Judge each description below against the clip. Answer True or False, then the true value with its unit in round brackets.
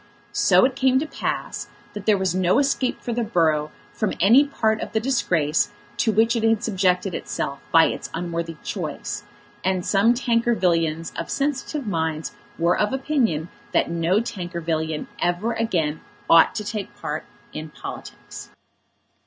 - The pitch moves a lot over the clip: True (5.8 semitones)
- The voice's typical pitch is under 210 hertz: True (190 Hz)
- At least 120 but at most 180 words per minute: True (155 wpm)